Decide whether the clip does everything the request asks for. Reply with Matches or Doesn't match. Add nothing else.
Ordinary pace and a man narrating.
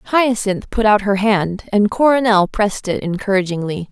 Doesn't match